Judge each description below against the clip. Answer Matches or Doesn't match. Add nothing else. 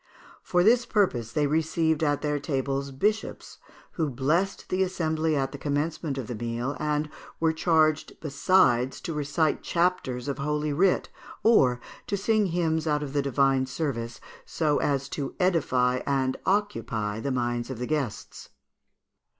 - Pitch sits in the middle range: Matches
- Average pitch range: Matches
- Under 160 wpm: Matches